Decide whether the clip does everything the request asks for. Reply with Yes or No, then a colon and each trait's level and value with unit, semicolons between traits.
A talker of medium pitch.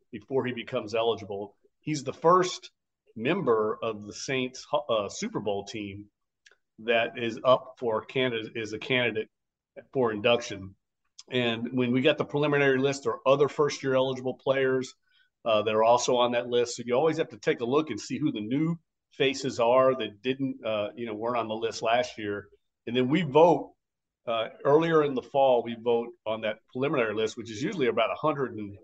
No: low, 120 Hz